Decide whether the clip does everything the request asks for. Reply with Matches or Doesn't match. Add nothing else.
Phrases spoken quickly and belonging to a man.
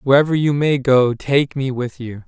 Matches